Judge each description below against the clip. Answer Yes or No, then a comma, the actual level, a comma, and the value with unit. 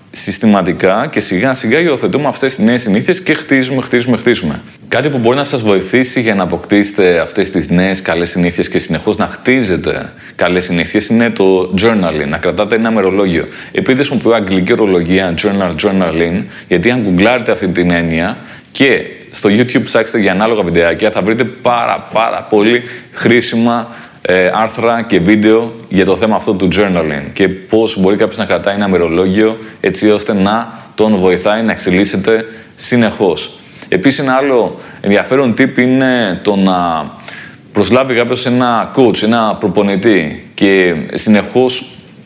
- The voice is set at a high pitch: No, low, 110 Hz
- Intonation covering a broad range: No, average, 4.4 semitones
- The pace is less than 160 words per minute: Yes, average, 150 wpm